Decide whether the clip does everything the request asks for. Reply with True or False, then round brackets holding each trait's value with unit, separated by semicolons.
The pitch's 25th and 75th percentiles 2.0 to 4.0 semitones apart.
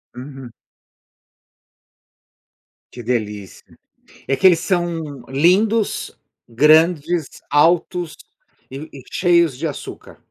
False (4.6 semitones)